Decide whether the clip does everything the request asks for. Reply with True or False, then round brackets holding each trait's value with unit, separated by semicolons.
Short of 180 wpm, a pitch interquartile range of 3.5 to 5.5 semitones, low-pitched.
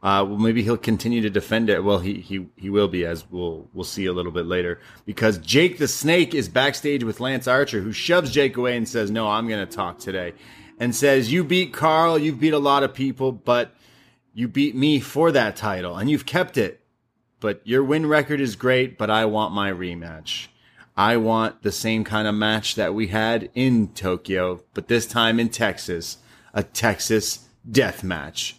False (205 wpm; 4.4 semitones; 115 Hz)